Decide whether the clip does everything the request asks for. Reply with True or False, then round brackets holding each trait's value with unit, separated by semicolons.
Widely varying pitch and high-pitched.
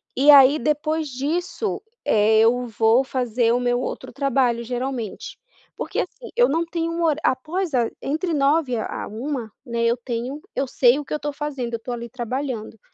False (4.1 semitones; 260 Hz)